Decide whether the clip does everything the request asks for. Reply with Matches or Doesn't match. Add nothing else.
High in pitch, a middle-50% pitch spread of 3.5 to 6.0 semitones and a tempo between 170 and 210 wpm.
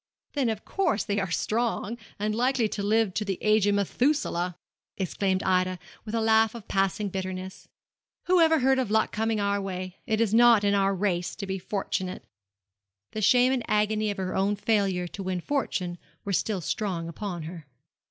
Doesn't match